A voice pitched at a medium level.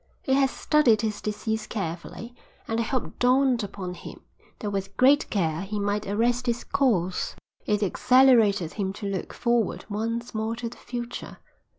No: high, 220 Hz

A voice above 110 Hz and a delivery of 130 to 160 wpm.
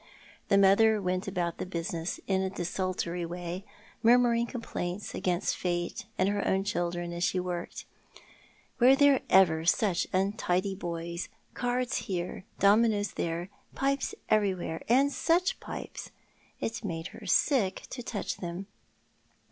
Yes: high, 190 Hz; average, 140 wpm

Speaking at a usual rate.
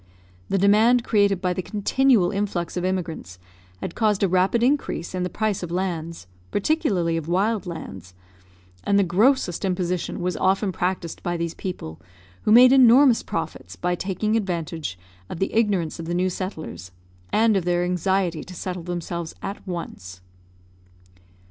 Yes: average, 155 wpm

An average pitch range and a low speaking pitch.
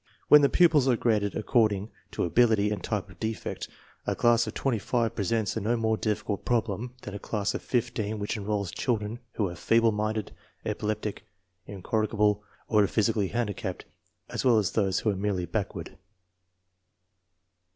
No: narrow, 2.2 semitones; low, 110 Hz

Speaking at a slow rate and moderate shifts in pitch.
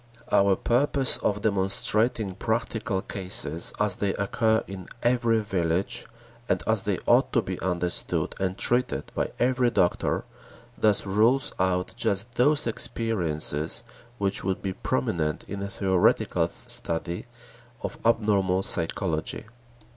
Yes: slow, 125 wpm; average, 3.8 semitones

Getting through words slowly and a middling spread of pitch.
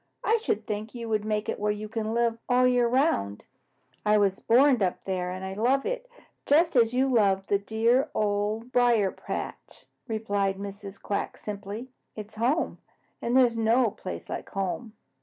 No: average, 185 wpm; average, 3.4 semitones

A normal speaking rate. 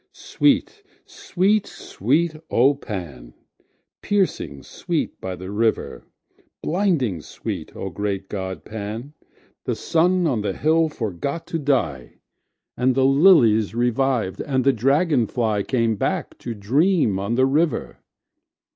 No: slow, 110 wpm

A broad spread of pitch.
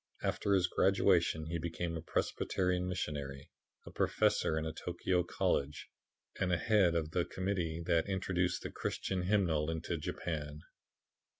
No: narrow, 2.5 semitones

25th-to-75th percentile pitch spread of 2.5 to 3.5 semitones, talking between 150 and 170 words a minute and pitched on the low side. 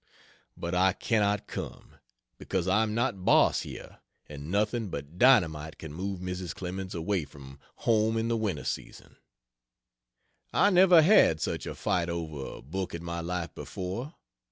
No: average, 4.5 semitones; average, 155 wpm; very low, 95 Hz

